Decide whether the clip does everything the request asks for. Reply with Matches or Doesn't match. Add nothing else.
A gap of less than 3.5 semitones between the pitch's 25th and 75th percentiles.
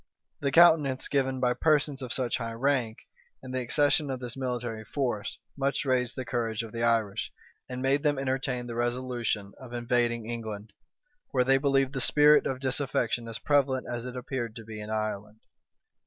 Matches